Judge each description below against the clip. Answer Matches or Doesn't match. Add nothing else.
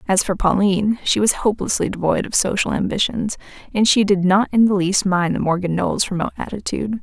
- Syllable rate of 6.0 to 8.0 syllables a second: Matches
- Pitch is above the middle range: Matches